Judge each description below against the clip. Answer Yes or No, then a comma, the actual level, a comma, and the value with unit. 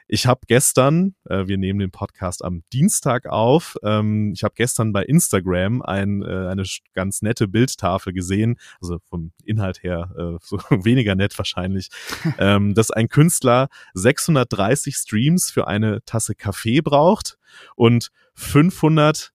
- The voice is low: Yes, low, 110 Hz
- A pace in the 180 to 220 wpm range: No, average, 145 wpm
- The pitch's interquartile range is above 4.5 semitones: Yes, average, 5.0 semitones